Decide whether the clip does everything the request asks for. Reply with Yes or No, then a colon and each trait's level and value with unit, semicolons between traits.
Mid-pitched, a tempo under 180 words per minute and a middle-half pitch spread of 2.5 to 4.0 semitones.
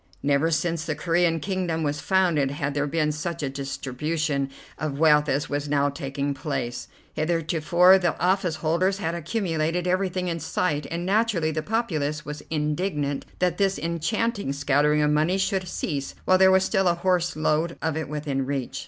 Yes: medium, 160 Hz; average, 170 wpm; average, 3.5 semitones